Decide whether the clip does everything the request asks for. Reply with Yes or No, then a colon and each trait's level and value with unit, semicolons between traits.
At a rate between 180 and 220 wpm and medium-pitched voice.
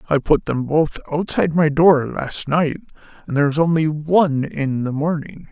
Yes: average, 185 wpm; medium, 150 Hz